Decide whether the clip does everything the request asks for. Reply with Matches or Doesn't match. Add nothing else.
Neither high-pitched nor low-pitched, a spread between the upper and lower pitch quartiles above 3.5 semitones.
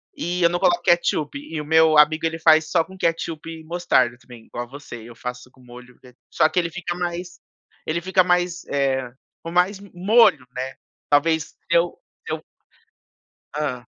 Matches